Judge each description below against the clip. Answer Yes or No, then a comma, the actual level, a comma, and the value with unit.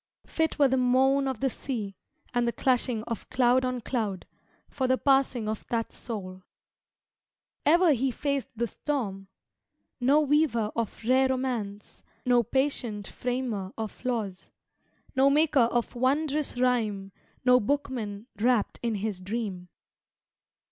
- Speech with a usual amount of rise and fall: Yes, average, 3.6 semitones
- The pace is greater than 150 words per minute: No, slow, 135 wpm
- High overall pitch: Yes, high, 245 Hz